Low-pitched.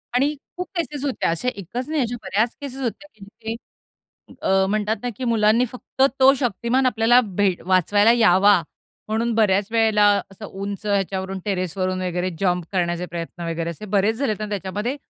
No: high, 210 Hz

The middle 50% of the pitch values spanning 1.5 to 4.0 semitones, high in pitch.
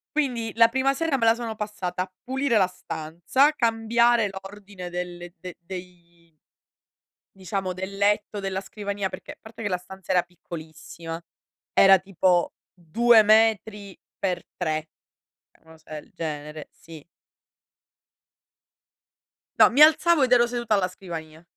No: average, 4.4 semitones; high, 195 Hz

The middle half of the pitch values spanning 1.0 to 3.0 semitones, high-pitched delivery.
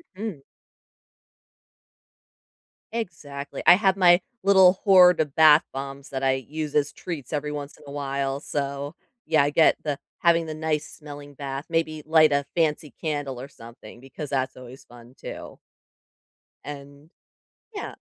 No: narrow, 2.5 semitones; medium, 145 Hz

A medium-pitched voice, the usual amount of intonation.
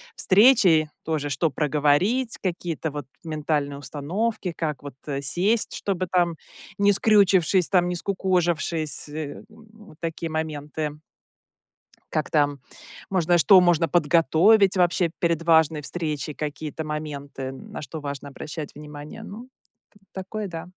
Yes: medium, 160 Hz; average, 3.8 semitones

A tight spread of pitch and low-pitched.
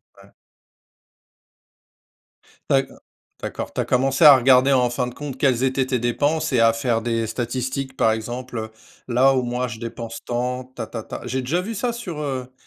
Yes: narrow, 2.2 semitones; low, 125 Hz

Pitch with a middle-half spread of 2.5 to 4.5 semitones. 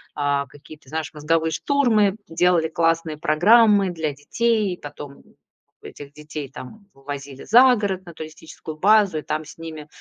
No: average, 5.0 semitones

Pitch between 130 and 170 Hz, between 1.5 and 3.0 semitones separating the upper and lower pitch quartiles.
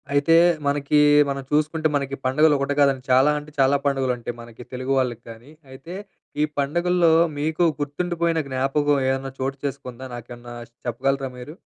Yes: medium, 140 Hz; narrow, 2.5 semitones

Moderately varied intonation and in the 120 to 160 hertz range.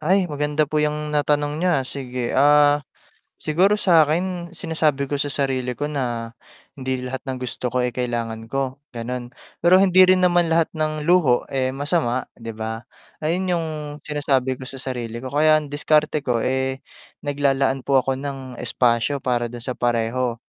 Yes: average, 3.3 semitones; medium, 140 Hz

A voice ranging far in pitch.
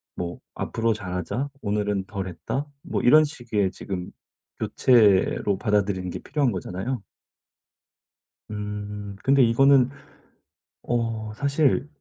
No: average, 4.6 semitones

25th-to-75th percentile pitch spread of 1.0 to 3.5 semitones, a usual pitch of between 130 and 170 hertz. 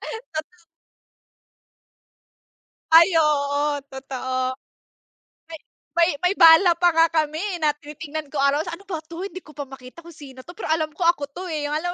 No: average, 3.0 semitones; very high, 315 Hz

